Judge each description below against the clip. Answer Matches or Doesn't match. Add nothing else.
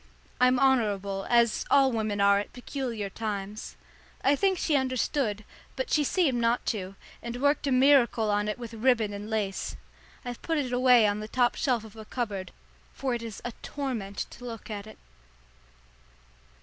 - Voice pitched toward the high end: Matches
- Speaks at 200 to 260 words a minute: Doesn't match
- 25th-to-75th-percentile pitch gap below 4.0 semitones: Matches